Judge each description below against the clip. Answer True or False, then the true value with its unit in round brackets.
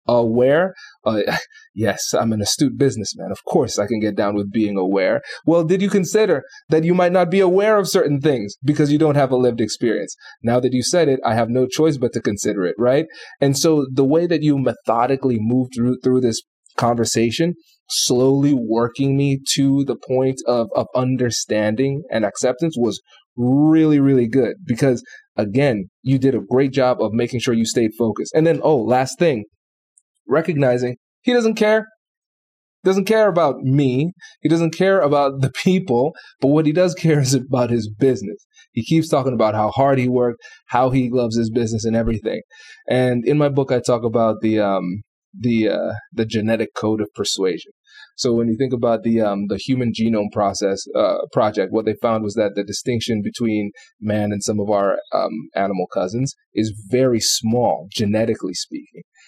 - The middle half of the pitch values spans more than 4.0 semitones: True (4.7 semitones)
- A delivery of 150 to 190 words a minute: True (185 wpm)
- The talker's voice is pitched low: True (125 Hz)